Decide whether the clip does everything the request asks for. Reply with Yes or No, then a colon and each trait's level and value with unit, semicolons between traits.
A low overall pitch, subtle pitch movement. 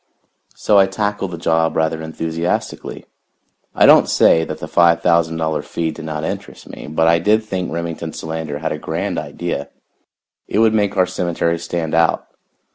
Yes: very low, 85 Hz; narrow, 2.0 semitones